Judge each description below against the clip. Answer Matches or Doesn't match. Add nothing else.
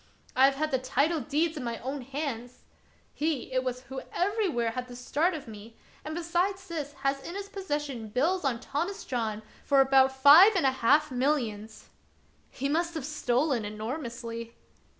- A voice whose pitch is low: Doesn't match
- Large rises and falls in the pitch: Doesn't match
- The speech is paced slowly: Doesn't match